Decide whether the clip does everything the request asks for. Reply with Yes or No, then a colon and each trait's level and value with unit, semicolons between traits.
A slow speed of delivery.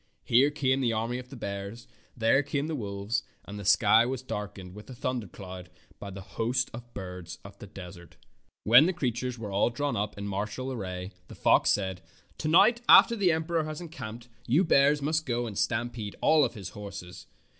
No: average, 190 wpm